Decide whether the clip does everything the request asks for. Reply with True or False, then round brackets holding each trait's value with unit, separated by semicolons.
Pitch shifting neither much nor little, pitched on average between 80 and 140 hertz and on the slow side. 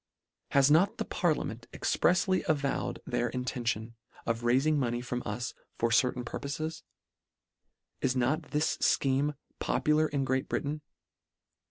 True (3.8 semitones; 135 Hz; 130 wpm)